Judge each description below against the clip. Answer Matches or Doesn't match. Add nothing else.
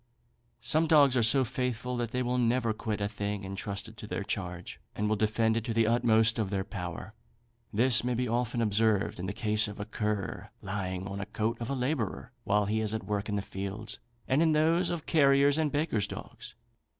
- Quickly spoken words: Matches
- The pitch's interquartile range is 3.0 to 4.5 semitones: Matches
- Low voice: Matches